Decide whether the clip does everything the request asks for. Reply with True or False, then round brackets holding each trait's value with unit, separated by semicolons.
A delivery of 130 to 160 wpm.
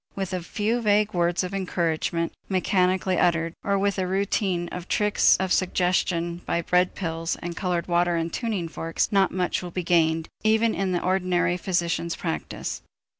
False (170 wpm)